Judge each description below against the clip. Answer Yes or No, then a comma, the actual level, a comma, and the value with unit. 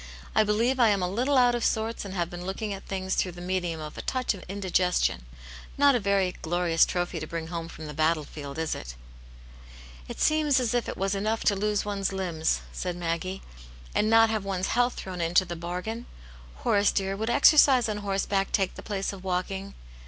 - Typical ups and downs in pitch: Yes, average, 3.8 semitones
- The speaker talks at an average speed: No, fast, 215 wpm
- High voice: Yes, high, 195 Hz